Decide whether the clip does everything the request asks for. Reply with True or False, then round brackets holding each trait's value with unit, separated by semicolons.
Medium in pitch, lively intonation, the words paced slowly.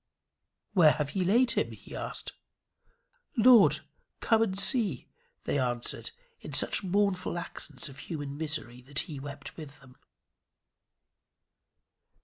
True (155 Hz; 6.0 semitones; 125 wpm)